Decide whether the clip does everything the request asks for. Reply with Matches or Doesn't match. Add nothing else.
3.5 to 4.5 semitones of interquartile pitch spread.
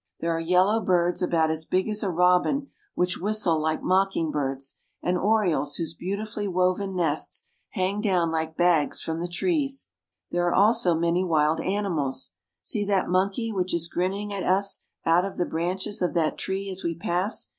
Doesn't match